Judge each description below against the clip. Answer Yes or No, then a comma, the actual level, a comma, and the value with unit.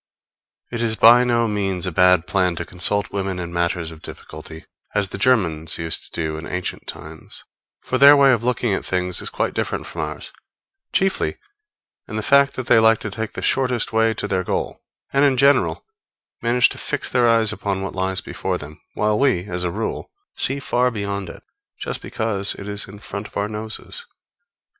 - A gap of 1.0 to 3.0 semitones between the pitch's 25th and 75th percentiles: No, average, 4.5 semitones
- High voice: No, low, 105 Hz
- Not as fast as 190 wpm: No, average, 200 wpm